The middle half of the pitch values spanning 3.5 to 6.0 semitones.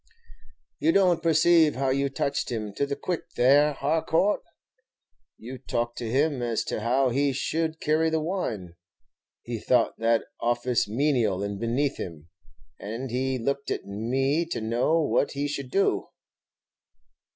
Yes: average, 4.6 semitones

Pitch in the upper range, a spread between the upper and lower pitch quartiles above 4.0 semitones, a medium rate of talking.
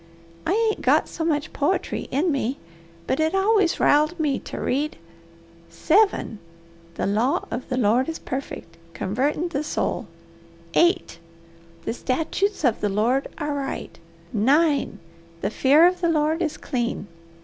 Yes: very high, 295 Hz; average, 4.7 semitones; average, 145 wpm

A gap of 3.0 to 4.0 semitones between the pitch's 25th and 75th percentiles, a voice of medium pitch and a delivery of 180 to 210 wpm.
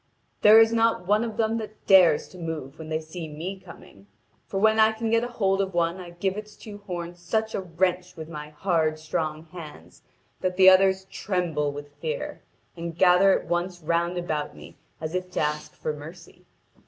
Yes: average, 3.6 semitones; medium, 180 Hz; average, 195 wpm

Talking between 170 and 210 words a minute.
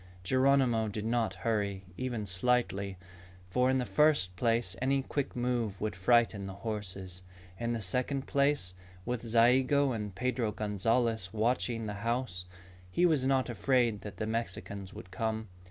No: average, 150 wpm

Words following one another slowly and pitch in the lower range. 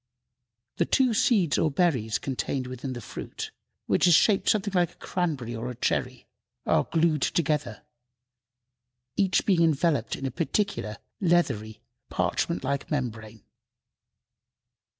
No: slow, 130 wpm; medium, 145 Hz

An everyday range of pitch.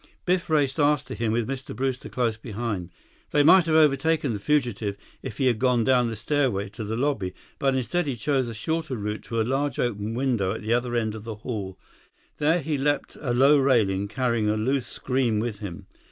Yes: average, 4.2 semitones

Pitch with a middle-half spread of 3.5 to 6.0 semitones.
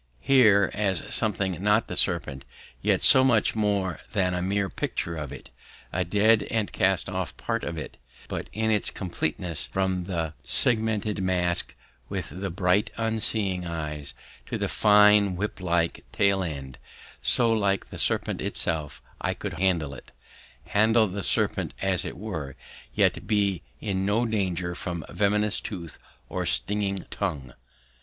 No: average, 3.1 semitones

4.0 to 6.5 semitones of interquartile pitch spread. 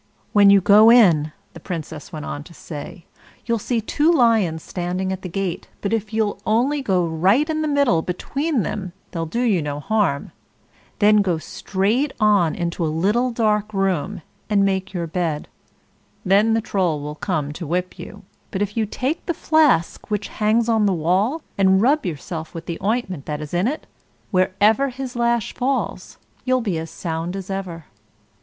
Yes: average, 4.9 semitones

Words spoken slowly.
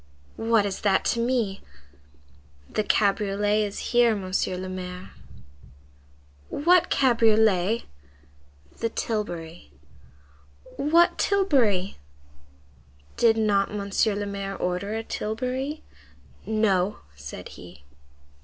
Yes: slow, 95 wpm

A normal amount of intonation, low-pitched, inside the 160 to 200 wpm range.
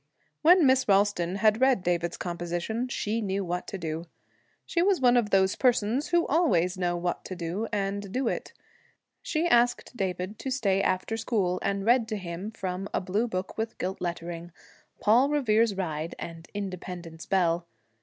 No: average, 4.6 semitones; high, 195 Hz; average, 170 wpm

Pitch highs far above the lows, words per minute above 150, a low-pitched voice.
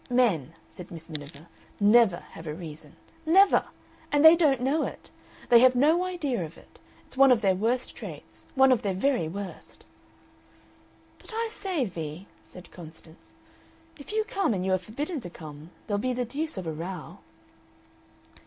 No: wide, 8.7 semitones; average, 170 wpm; high, 220 Hz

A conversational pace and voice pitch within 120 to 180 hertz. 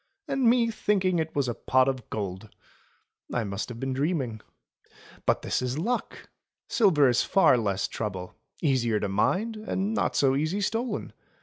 Yes: average, 170 wpm; low, 135 Hz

